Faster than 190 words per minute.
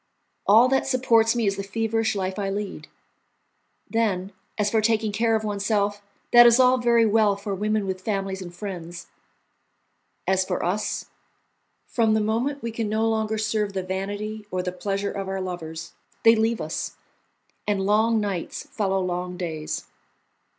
No: average, 165 wpm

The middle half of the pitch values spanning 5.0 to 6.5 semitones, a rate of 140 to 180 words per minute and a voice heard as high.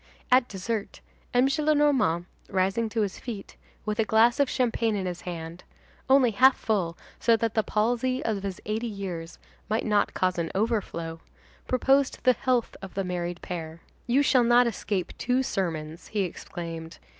Yes: average, 5.3 semitones; average, 155 wpm; high, 215 Hz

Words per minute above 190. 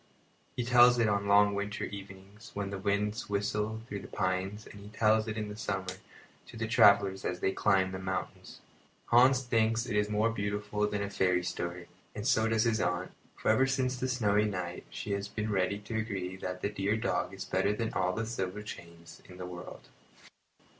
Yes: fast, 205 wpm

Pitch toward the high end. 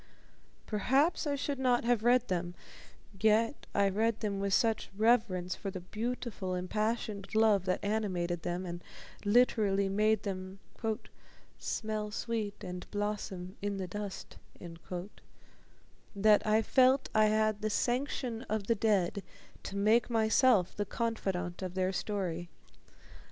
Yes: high, 210 Hz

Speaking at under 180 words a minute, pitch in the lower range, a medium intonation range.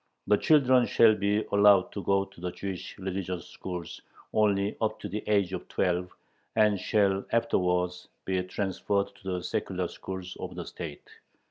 No: average, 160 wpm; very low, 95 Hz; narrow, 2.3 semitones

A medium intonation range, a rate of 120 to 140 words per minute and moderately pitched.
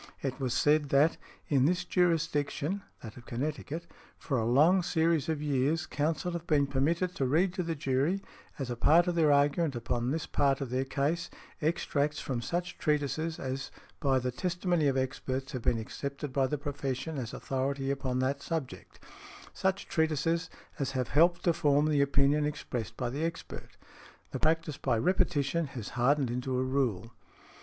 No: average, 3.7 semitones; average, 175 wpm; medium, 145 Hz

